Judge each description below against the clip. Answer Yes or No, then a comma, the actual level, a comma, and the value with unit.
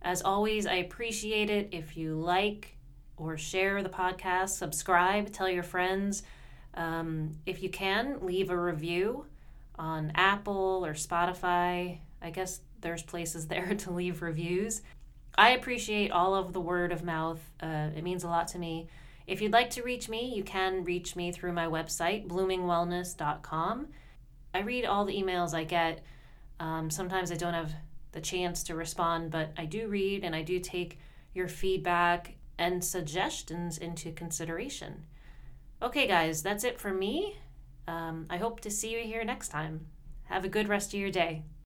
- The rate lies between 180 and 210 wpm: No, average, 165 wpm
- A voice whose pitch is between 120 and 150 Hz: No, medium, 175 Hz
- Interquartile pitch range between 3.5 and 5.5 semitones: No, average, 2.7 semitones